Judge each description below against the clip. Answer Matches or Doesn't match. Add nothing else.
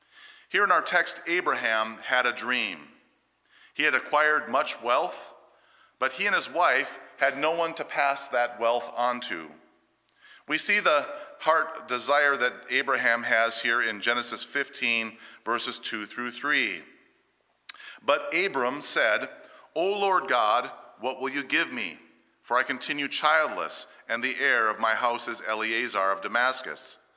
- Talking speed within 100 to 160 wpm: Matches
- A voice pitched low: Matches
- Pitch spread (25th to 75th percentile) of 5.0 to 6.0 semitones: Doesn't match